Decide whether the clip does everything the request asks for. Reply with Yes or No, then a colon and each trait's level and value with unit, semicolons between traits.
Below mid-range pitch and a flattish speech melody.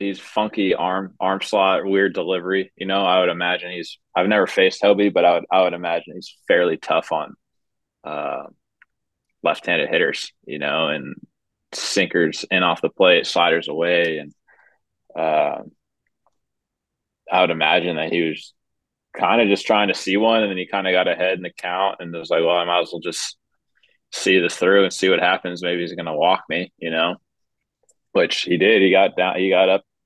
Yes: very low, 95 Hz; narrow, 1.7 semitones